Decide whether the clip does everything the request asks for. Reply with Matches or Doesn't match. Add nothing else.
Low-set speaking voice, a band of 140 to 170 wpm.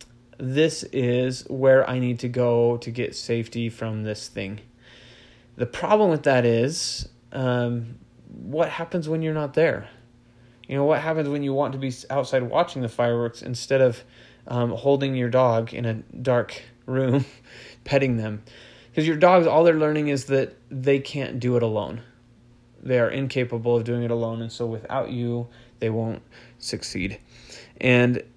Matches